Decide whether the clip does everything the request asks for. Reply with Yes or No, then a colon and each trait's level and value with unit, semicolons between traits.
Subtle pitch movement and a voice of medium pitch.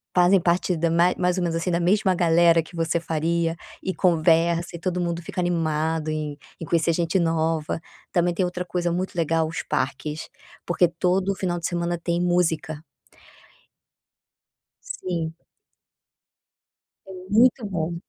Yes: narrow, 1.6 semitones; medium, 170 Hz